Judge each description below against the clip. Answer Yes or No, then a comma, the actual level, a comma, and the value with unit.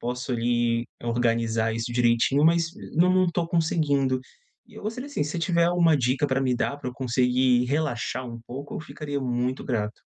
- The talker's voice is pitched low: Yes, low, 130 Hz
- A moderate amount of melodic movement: Yes, average, 4.6 semitones